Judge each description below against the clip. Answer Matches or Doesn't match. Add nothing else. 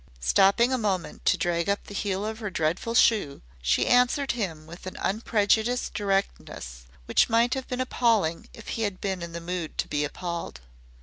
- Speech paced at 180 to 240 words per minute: Matches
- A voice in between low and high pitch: Doesn't match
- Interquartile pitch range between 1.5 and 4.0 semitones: Doesn't match